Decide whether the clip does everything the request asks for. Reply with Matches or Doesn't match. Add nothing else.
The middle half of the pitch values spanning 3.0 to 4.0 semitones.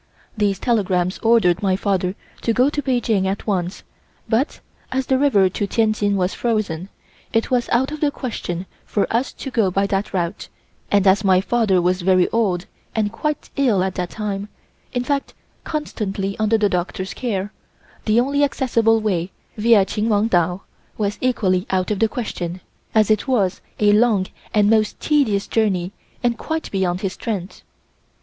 Matches